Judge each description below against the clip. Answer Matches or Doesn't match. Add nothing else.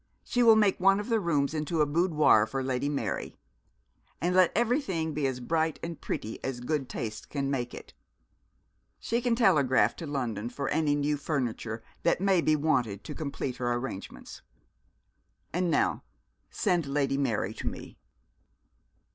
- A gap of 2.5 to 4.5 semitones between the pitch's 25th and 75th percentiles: Doesn't match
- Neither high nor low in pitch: Matches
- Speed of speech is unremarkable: Matches